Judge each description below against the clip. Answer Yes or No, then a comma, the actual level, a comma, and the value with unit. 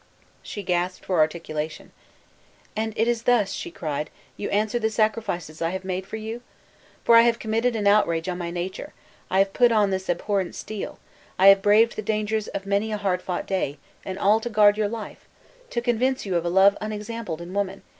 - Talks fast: Yes, fast, 210 wpm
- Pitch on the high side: Yes, high, 200 Hz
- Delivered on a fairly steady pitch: No, average, 3.2 semitones